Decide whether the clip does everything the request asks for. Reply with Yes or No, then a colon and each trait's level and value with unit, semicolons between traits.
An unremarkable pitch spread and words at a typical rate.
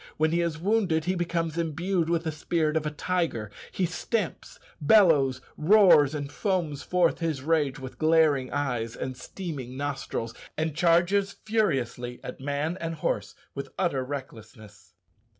Yes: average, 4.3 semitones; average, 150 wpm